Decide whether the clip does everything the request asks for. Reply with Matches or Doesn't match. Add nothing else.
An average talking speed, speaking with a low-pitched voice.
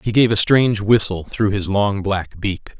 Doesn't match